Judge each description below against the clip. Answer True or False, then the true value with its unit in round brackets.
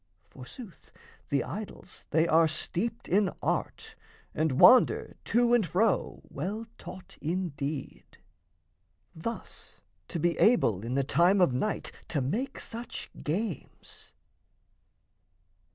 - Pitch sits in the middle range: True (175 Hz)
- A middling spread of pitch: False (6.4 semitones)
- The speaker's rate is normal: False (110 wpm)